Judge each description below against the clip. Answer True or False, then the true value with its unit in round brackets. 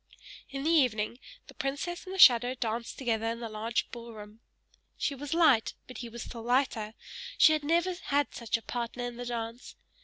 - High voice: True (245 Hz)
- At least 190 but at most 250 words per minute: True (195 wpm)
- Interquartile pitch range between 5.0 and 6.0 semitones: False (3.6 semitones)